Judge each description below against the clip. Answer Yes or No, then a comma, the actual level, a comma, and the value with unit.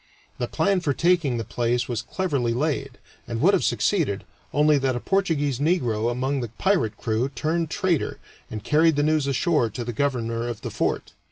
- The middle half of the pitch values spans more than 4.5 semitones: Yes, average, 5.1 semitones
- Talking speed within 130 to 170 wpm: No, average, 185 wpm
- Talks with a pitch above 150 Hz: No, medium, 140 Hz